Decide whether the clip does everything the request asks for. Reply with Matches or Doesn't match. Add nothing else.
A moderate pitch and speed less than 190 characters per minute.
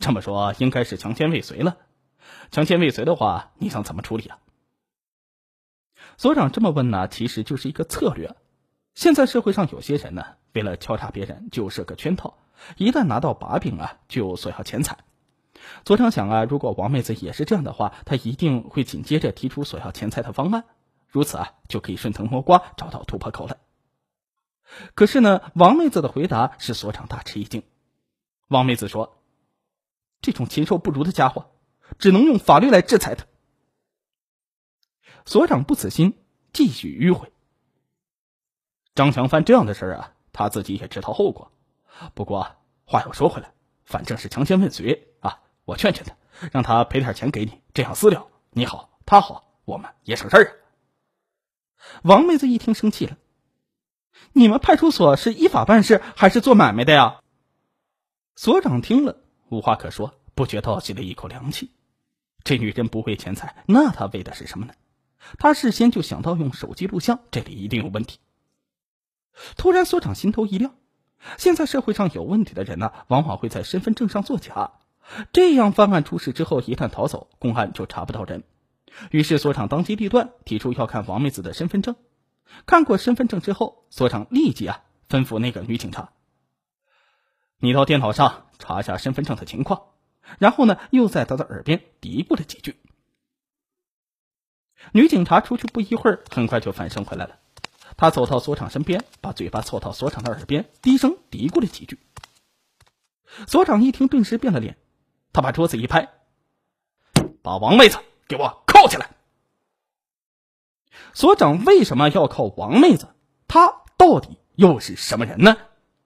Doesn't match